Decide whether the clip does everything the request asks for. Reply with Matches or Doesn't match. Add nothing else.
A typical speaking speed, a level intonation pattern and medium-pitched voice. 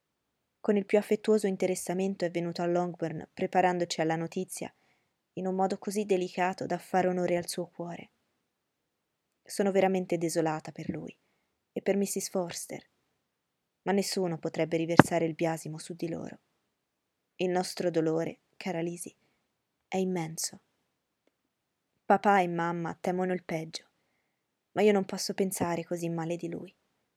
Matches